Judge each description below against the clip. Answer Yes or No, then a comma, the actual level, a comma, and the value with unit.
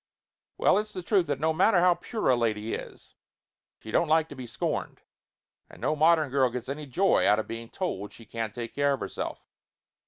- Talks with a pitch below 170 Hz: Yes, medium, 140 Hz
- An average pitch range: No, wide, 6.5 semitones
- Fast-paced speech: Yes, fast, 210 wpm